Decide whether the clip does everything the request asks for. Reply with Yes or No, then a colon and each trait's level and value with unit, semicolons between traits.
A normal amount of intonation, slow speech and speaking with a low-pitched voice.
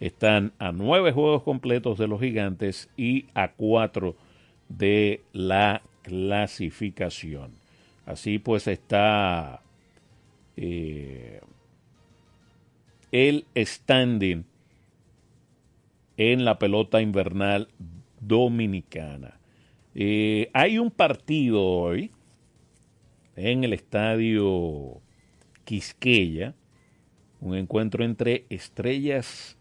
Yes: average, 4.2 semitones; slow, 75 wpm; low, 105 Hz